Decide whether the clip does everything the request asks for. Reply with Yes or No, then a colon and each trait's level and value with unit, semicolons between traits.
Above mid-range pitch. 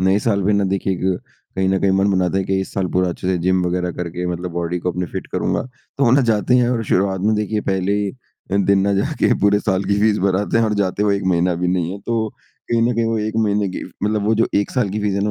No: low, 100 Hz